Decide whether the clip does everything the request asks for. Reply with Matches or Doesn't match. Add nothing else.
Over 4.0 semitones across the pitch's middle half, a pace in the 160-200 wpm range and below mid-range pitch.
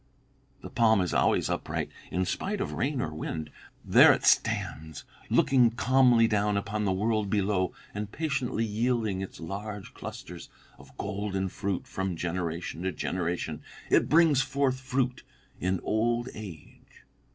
Doesn't match